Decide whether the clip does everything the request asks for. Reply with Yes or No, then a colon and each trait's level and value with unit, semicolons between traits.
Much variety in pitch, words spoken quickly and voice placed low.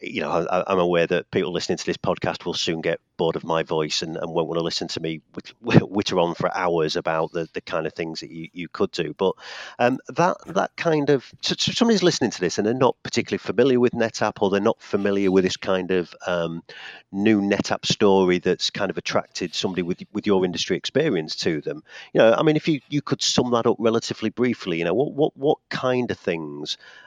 Yes: wide, 6.1 semitones; fast, 235 wpm; low, 100 Hz